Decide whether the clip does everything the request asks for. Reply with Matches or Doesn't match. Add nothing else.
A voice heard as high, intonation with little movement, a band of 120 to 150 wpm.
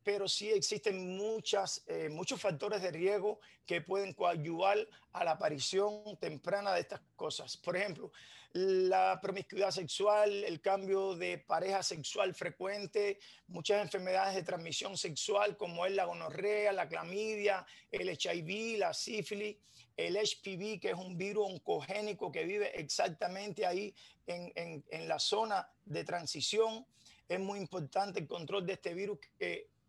Matches